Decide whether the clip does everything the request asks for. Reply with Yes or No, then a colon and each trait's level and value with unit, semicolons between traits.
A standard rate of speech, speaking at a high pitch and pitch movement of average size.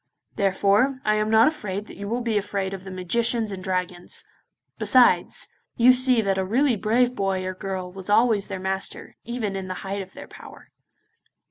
Yes: average, 190 wpm; high, 200 Hz; average, 3.4 semitones